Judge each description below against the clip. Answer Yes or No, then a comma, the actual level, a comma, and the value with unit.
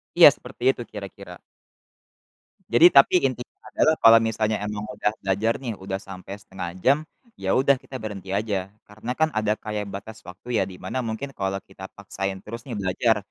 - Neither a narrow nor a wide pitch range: Yes, average, 3.4 semitones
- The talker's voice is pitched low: Yes, low, 105 Hz